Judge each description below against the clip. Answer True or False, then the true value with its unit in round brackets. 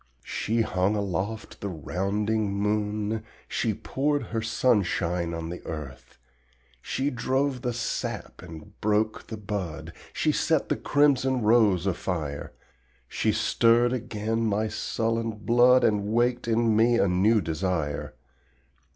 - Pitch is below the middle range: True (105 Hz)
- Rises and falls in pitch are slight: False (3.9 semitones)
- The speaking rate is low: True (125 wpm)